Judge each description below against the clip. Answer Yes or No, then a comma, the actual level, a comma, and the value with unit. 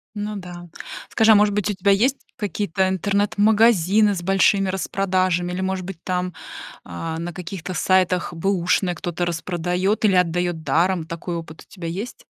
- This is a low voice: No, medium, 185 Hz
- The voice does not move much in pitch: Yes, narrow, 2.3 semitones